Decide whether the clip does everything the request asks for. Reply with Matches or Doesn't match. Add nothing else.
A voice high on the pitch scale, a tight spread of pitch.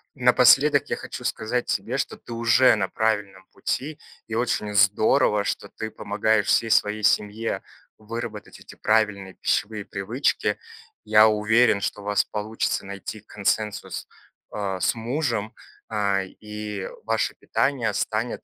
Doesn't match